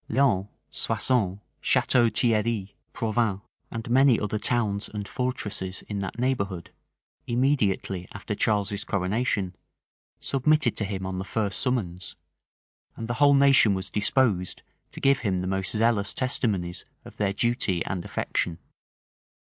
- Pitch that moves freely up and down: No, average, 4.0 semitones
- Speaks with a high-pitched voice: No, low, 105 Hz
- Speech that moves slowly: Yes, slow, 130 wpm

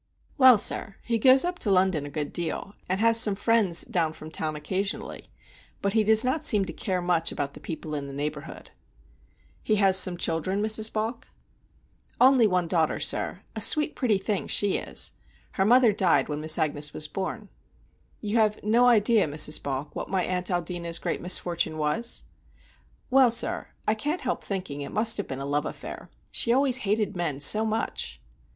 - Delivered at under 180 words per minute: No, average, 185 wpm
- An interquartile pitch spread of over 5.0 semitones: Yes, wide, 5.6 semitones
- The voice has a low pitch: No, high, 195 Hz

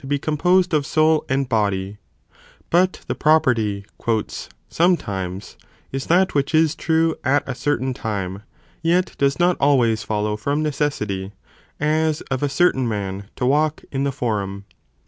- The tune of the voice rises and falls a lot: Yes, wide, 6.7 semitones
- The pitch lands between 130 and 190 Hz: Yes, medium, 140 Hz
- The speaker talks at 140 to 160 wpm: Yes, average, 145 wpm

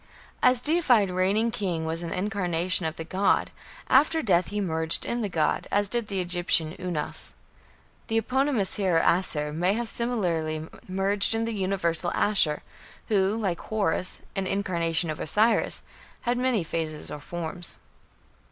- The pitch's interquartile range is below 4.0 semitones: No, average, 4.6 semitones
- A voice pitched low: No, high, 190 Hz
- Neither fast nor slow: Yes, average, 150 wpm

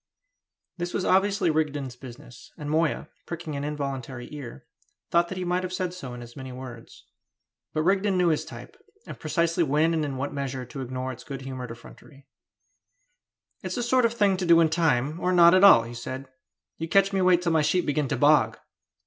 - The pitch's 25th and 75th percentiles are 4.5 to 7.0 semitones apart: Yes, average, 5.2 semitones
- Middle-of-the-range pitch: Yes, medium, 155 Hz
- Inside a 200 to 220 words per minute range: Yes, fast, 205 wpm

